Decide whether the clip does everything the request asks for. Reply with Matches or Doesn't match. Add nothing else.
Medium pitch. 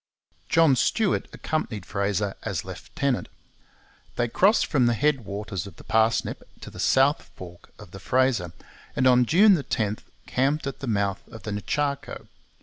Doesn't match